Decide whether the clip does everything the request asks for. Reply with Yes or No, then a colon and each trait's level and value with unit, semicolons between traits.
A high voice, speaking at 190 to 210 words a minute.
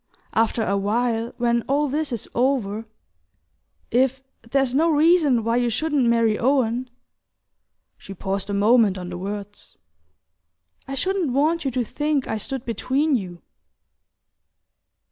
No: high, 245 Hz; average, 140 wpm